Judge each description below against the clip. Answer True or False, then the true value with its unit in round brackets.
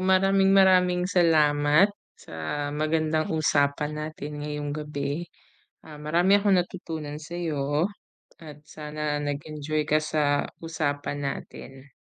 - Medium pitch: True (155 Hz)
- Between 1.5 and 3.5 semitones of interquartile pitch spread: True (2.8 semitones)